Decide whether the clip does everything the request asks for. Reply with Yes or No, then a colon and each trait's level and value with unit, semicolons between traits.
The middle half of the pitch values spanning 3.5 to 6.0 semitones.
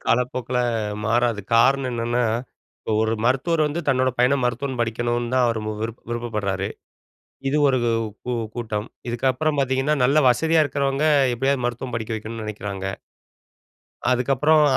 No: average, 2.9 semitones